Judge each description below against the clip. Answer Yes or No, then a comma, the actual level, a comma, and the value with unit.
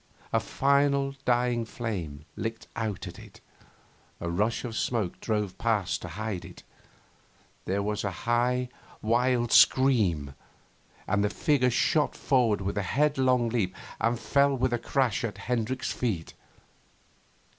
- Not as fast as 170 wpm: Yes, slow, 135 wpm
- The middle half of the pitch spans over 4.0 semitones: No, average, 3.7 semitones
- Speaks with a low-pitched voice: Yes, low, 115 Hz